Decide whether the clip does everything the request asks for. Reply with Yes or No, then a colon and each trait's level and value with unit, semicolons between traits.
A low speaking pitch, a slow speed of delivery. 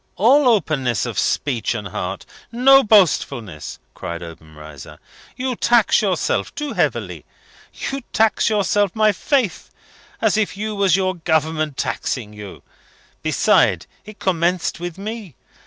No: medium, 185 Hz; slow, 125 wpm